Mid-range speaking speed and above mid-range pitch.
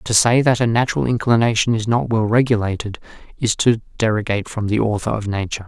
No: average, 190 wpm; low, 110 Hz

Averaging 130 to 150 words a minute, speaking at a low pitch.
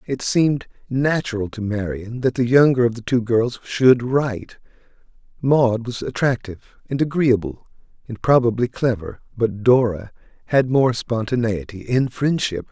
Yes: slow, 135 wpm; low, 120 Hz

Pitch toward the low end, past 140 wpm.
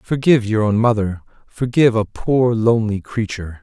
No: low, 110 Hz; slow, 135 wpm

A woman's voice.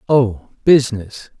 No: male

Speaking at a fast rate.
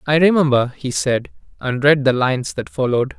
No: average, 170 wpm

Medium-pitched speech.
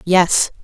Yes: medium, 180 Hz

